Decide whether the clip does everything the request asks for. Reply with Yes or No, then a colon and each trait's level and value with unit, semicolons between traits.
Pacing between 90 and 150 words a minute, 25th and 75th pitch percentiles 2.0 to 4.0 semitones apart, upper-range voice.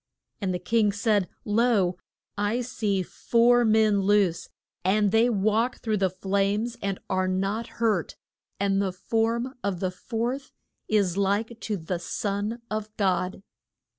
Yes: average, 140 wpm; average, 2.8 semitones; high, 205 Hz